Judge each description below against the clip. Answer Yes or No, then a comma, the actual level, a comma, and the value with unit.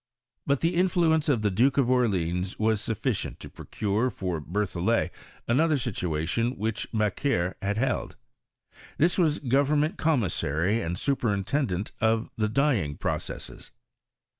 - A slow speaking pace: Yes, slow, 130 wpm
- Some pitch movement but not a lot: No, wide, 6.1 semitones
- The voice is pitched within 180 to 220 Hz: No, low, 115 Hz